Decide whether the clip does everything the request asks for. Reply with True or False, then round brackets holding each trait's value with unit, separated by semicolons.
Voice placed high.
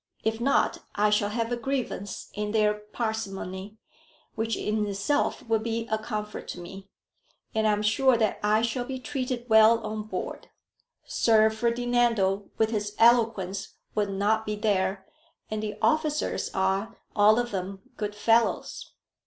True (215 Hz)